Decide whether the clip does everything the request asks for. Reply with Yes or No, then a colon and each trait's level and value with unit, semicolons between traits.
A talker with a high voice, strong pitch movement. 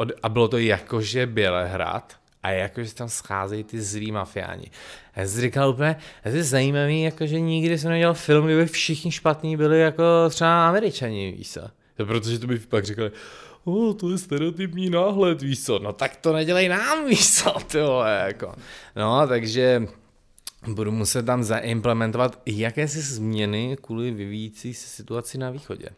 No: low, 125 Hz; wide, 6.4 semitones